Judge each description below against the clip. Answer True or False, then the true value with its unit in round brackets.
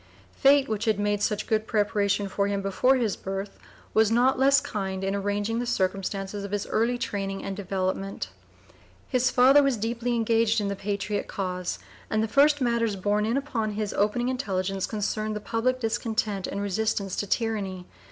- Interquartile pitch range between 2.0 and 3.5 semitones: True (2.9 semitones)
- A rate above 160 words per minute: True (175 wpm)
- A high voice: True (210 Hz)